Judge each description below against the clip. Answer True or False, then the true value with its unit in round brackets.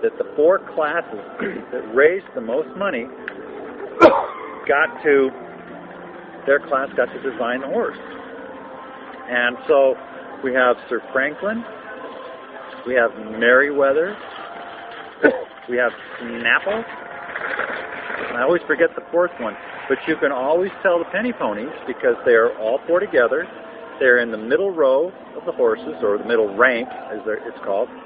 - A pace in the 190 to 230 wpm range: False (140 wpm)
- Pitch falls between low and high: False (220 Hz)